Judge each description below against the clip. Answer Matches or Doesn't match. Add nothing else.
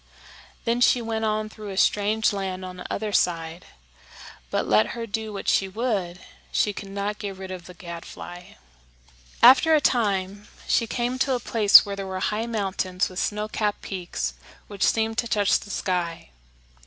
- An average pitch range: Matches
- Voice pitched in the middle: Doesn't match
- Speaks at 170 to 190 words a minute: Matches